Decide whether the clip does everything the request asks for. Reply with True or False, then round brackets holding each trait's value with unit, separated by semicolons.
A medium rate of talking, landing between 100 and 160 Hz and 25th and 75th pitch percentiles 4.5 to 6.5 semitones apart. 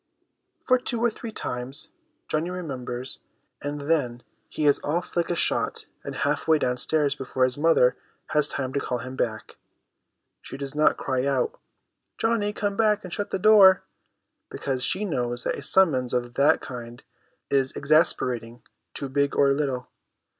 True (170 wpm; 140 Hz; 5.3 semitones)